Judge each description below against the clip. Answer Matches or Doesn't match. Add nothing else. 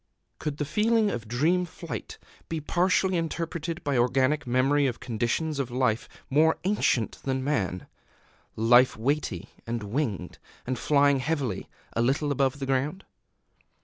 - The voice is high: Doesn't match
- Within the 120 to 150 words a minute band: Matches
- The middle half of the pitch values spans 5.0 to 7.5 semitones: Doesn't match